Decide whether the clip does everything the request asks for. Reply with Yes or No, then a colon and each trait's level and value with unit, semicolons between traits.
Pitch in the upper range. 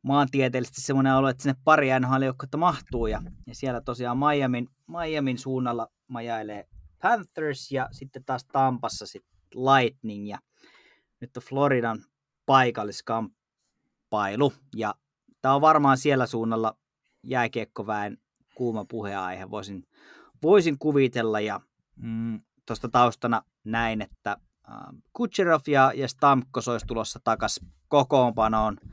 No: low, 125 Hz